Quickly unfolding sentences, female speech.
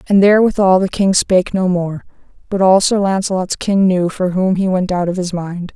Yes: fast, 220 wpm; female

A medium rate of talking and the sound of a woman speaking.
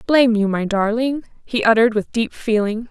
Yes: average, 185 wpm; female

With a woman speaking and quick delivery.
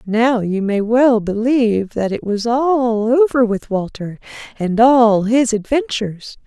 No: female; average, 150 wpm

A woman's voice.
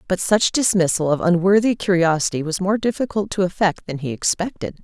Yes: female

